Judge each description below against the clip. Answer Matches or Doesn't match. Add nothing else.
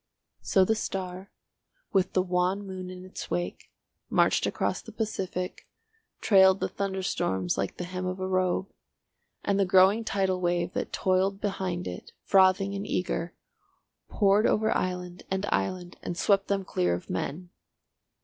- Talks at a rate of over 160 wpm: Doesn't match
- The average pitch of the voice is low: Doesn't match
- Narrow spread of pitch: Matches